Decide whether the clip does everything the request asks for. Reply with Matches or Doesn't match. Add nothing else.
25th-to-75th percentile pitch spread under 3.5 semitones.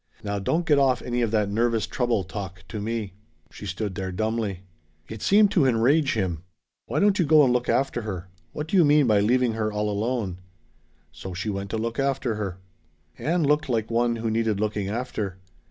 Doesn't match